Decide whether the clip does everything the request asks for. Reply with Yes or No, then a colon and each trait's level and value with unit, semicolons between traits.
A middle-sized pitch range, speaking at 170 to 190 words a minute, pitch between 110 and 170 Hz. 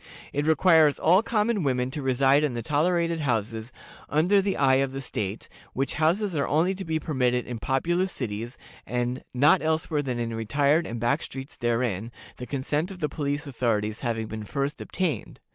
Yes: average, 4.8 semitones; average, 180 wpm; medium, 140 Hz